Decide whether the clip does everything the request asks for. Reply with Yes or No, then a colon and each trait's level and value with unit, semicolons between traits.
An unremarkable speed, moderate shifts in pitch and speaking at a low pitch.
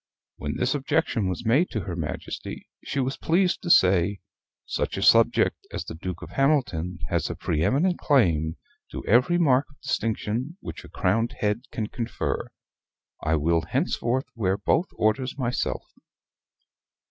No: average, 155 wpm; wide, 6.8 semitones; low, 115 Hz